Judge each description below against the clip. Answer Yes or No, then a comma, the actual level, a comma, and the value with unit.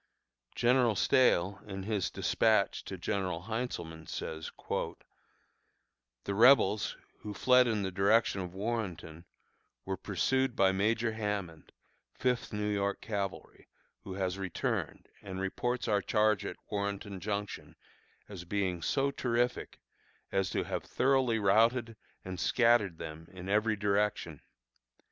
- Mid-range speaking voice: No, low, 100 Hz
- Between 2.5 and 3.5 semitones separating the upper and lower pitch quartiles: Yes, average, 3.2 semitones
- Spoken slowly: Yes, slow, 125 wpm